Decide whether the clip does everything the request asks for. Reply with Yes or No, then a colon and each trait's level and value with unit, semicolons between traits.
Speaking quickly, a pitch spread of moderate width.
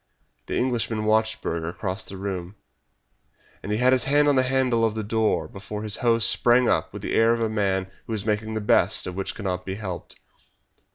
Yes: fast, 220 wpm; average, 3.0 semitones